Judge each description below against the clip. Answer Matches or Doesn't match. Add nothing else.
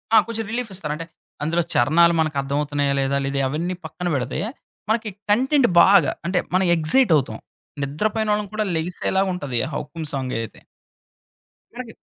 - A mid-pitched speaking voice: Matches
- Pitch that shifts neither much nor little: Doesn't match